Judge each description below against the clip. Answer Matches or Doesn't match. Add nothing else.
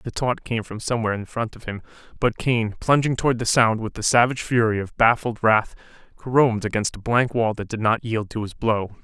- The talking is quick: Matches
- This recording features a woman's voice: Doesn't match